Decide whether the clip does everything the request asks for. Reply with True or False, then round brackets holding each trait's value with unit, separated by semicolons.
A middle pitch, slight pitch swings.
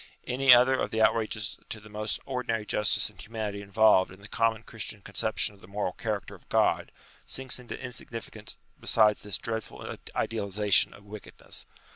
False (110 Hz; 1.8 semitones)